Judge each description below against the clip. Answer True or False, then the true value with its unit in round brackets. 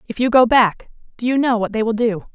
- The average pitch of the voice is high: True (230 Hz)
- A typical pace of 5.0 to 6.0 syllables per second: True (5.9 syllables/s)